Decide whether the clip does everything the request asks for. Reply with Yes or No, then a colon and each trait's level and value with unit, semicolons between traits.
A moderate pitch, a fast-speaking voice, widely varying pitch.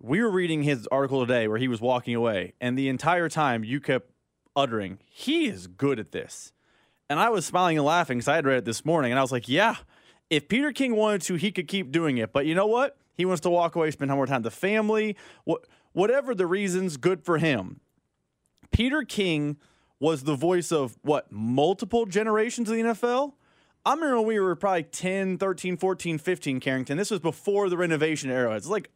Yes: medium, 165 Hz; fast, 220 wpm; wide, 6.5 semitones